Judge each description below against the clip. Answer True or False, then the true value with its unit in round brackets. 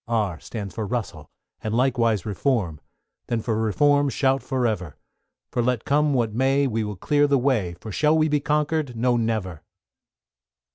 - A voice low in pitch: True (120 Hz)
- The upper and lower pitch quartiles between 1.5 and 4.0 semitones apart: False (4.5 semitones)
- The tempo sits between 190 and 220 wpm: False (170 wpm)